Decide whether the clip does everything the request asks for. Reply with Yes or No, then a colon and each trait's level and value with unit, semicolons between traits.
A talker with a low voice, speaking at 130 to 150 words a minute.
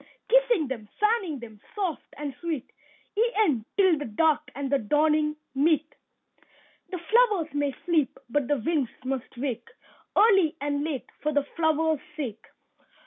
No: very high, 300 Hz; average, 140 wpm